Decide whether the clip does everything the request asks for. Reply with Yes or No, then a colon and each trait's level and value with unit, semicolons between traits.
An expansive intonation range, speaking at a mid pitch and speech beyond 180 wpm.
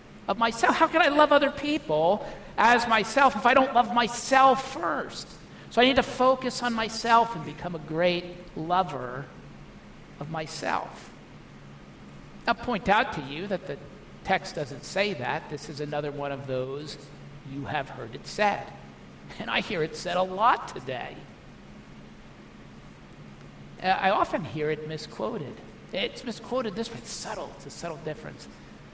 No: wide, 9.0 semitones; medium, 180 Hz; average, 155 wpm